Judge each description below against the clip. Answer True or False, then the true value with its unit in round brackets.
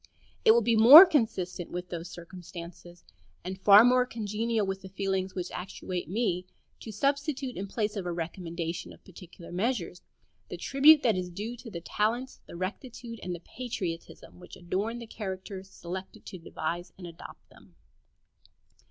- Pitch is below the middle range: False (190 Hz)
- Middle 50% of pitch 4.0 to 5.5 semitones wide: True (4.5 semitones)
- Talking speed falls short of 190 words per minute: True (160 wpm)